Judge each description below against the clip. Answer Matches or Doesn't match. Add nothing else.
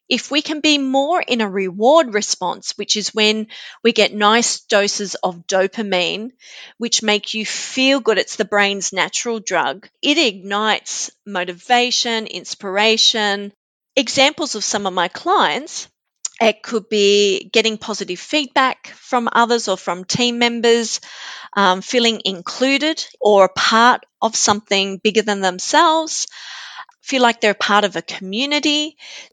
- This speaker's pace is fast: Doesn't match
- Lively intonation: Doesn't match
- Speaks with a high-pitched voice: Matches